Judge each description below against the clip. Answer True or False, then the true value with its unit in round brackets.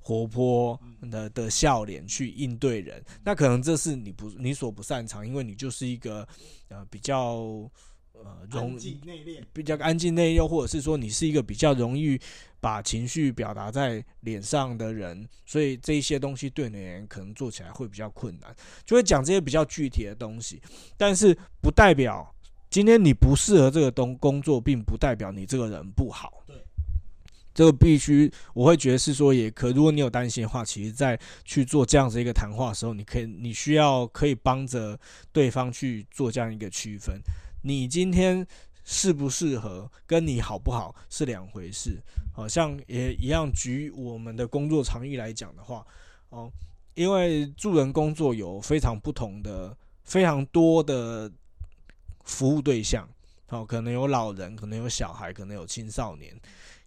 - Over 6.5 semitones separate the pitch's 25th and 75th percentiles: False (5.3 semitones)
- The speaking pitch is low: True (125 Hz)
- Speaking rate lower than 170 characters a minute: False (265 characters per minute)